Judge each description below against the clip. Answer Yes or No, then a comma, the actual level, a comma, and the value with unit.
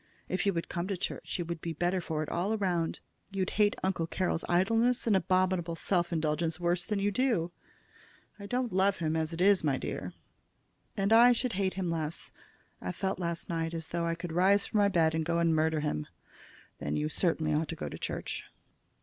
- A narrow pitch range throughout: No, average, 3.1 semitones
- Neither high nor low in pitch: Yes, medium, 175 Hz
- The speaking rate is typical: No, fast, 210 wpm